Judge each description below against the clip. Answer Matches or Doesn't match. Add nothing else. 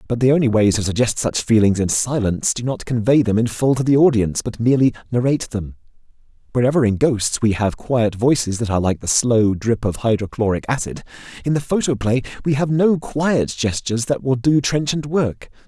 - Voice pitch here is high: Doesn't match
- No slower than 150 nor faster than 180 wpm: Doesn't match